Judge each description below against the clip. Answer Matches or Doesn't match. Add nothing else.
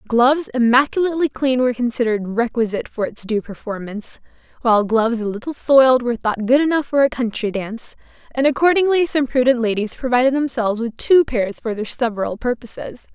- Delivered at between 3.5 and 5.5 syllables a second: Doesn't match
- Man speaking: Doesn't match